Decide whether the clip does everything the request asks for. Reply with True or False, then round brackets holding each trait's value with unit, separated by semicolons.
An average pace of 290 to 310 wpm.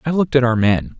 True (300 wpm)